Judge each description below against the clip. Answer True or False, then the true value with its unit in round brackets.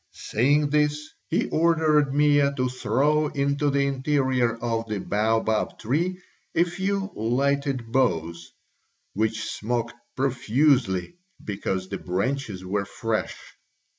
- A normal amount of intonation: True (5.0 semitones)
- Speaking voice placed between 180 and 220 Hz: False (130 Hz)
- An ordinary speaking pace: False (110 wpm)